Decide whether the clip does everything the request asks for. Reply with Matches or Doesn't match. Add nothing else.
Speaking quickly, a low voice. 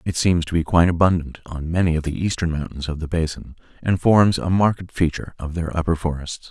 Matches